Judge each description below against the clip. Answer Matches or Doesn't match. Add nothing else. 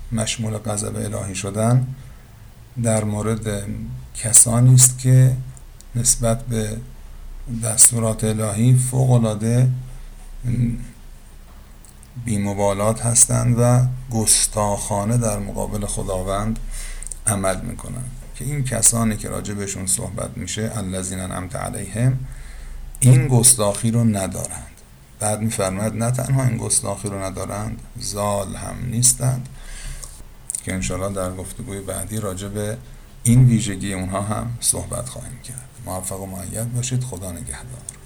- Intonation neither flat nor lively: Matches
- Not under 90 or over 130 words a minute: Matches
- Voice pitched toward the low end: Matches